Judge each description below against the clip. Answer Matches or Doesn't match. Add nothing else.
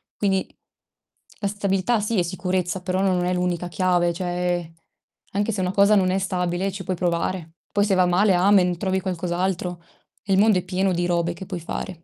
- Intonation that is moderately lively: Doesn't match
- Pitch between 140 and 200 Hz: Matches